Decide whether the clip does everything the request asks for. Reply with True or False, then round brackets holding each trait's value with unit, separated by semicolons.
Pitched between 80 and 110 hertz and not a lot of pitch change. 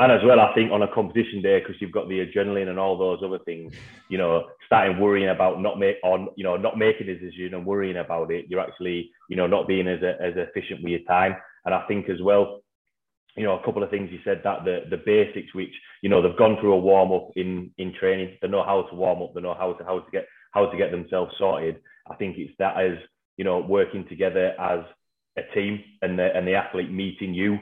True (95 Hz; 2.0 semitones)